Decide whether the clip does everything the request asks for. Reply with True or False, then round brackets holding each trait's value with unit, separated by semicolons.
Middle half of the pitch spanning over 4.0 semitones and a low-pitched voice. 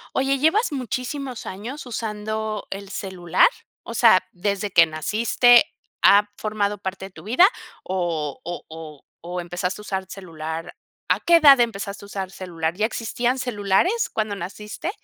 False (4.6 semitones; 205 Hz)